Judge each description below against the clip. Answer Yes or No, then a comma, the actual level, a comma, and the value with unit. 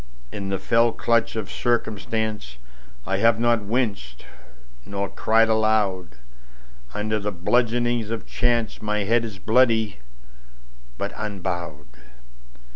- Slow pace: Yes, slow, 100 wpm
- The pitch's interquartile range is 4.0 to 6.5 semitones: Yes, average, 4.7 semitones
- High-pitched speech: No, low, 105 Hz